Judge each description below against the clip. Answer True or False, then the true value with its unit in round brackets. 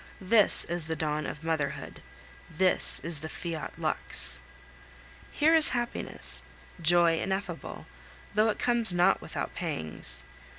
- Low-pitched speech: False (175 Hz)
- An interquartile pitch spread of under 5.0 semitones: True (4.2 semitones)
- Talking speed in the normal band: False (125 wpm)